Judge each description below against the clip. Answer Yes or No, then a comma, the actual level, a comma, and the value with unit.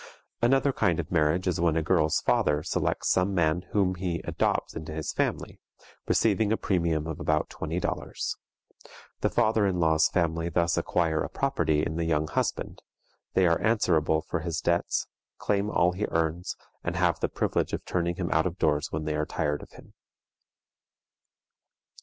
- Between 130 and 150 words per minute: No, average, 175 wpm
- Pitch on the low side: Yes, very low, 85 Hz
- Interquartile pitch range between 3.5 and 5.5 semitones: No, average, 2.7 semitones